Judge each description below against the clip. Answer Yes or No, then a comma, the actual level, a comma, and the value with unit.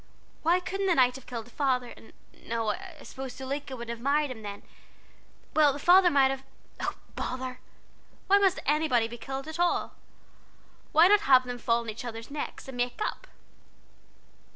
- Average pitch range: Yes, average, 4.5 semitones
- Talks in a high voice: Yes, very high, 265 Hz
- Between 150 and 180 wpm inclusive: Yes, average, 175 wpm